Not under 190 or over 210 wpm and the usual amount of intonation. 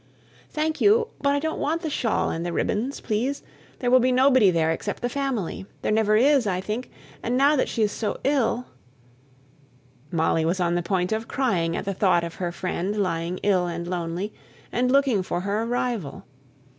No: average, 195 wpm; wide, 6.4 semitones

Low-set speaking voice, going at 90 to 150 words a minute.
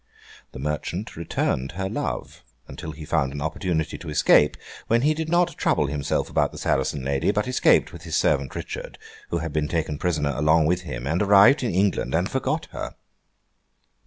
No: very low, 80 Hz; average, 185 wpm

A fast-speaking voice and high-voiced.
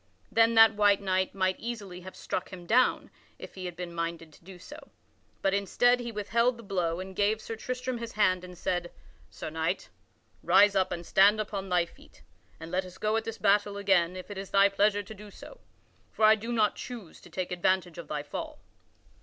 Yes: fast, 210 wpm; high, 195 Hz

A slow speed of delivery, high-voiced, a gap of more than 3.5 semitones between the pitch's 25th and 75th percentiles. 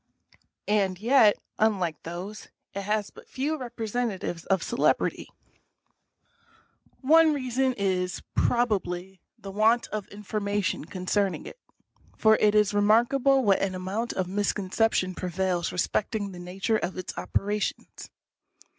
No: slow, 120 wpm; high, 205 Hz; average, 3.2 semitones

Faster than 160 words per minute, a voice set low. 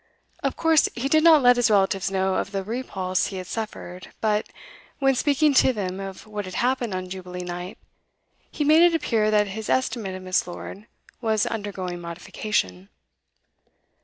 No: average, 170 wpm; high, 210 Hz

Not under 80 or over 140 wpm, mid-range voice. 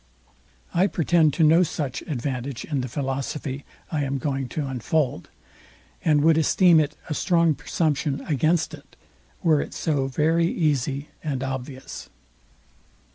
Yes: slow, 135 wpm; medium, 145 Hz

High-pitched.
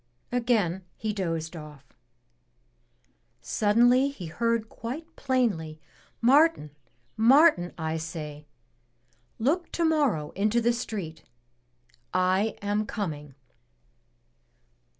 Yes: high, 210 Hz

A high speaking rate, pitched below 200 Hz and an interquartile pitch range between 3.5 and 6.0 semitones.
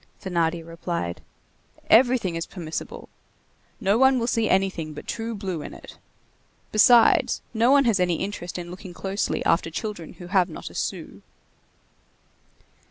No: average, 145 wpm; high, 190 Hz; average, 4.7 semitones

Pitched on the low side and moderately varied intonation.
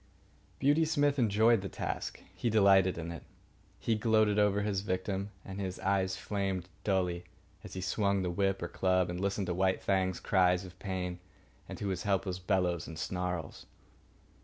No: very low, 95 Hz; narrow, 2.0 semitones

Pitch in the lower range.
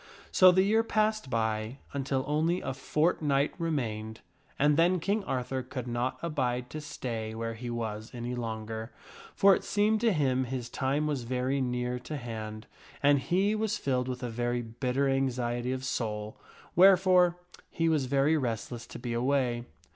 Yes: low, 130 Hz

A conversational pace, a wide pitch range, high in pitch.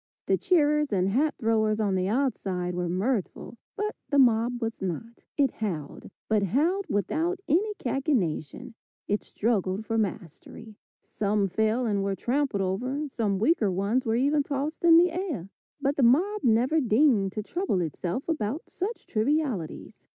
Yes: average, 155 wpm; wide, 6.6 semitones; high, 230 Hz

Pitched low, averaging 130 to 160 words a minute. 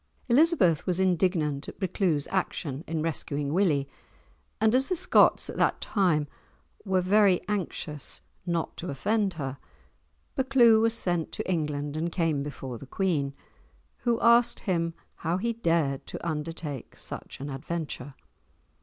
No: medium, 170 Hz; average, 140 wpm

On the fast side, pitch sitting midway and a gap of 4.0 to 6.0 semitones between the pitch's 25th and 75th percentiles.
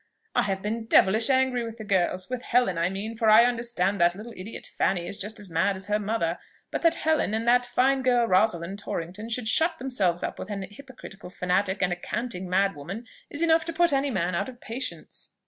No: fast, 220 wpm; high, 215 Hz; average, 4.6 semitones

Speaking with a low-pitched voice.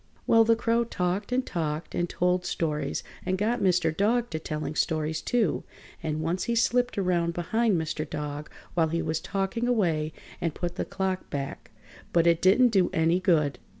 No: medium, 175 Hz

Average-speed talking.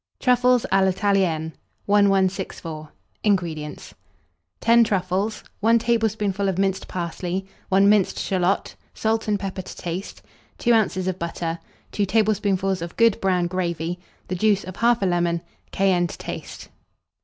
No: slow, 130 wpm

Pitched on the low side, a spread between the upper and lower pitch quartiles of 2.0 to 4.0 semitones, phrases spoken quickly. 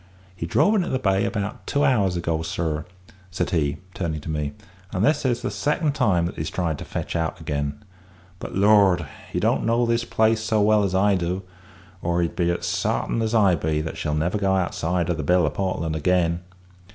No: very low, 90 Hz; average, 4.7 semitones; fast, 210 wpm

